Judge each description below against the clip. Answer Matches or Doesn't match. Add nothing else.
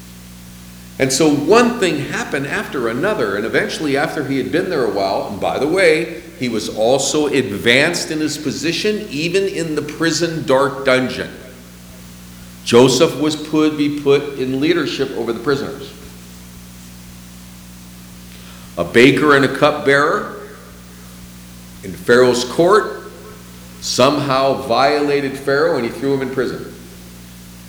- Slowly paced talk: Matches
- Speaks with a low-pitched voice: Matches